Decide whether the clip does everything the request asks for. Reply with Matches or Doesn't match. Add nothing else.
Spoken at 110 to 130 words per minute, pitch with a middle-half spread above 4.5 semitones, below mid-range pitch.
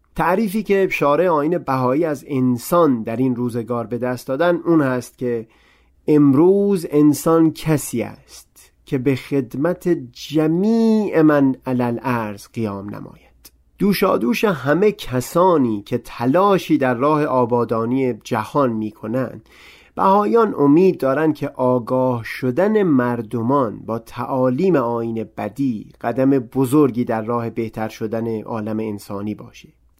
Matches